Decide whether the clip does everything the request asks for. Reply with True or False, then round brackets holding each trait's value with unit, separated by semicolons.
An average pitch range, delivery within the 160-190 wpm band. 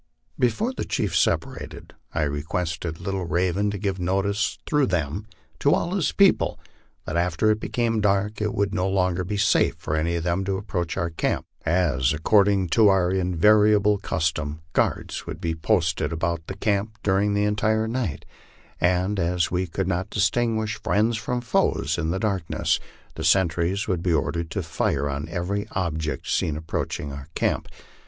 True (4.0 semitones; 170 wpm)